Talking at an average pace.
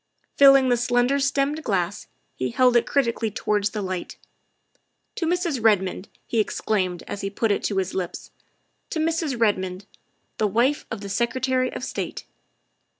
Yes: average, 170 wpm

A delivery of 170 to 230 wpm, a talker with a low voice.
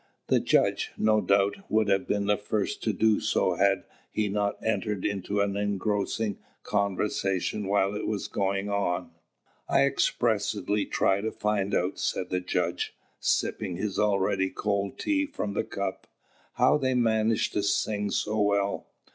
No: average, 155 wpm; low, 100 Hz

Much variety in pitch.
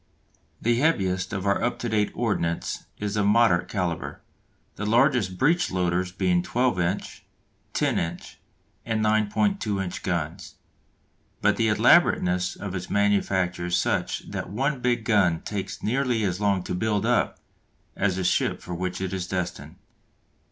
No: average, 3.5 semitones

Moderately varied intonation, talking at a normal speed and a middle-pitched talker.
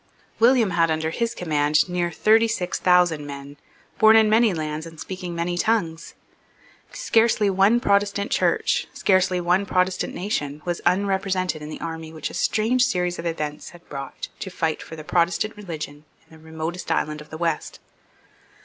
Yes: average, 4.0 semitones; average, 165 wpm; medium, 175 Hz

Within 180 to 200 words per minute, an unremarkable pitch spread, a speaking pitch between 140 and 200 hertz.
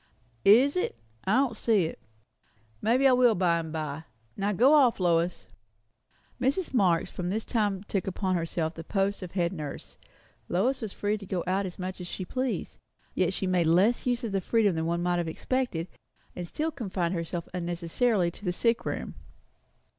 Yes: average, 185 wpm; average, 4.9 semitones; high, 190 Hz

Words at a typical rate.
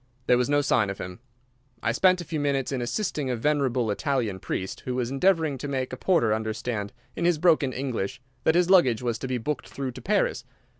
No: fast, 215 wpm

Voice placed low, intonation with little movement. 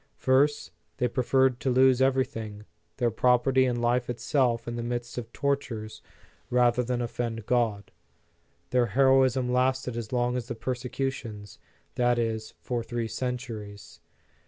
Yes: low, 120 Hz; narrow, 1.9 semitones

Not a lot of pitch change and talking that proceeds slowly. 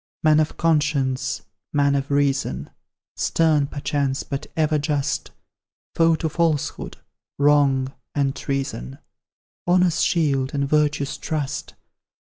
Yes: narrow, 2.1 semitones; slow, 110 wpm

